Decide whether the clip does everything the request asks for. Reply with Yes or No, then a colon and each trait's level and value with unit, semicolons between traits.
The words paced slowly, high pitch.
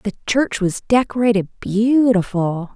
Yes: slow, 110 wpm; high, 215 Hz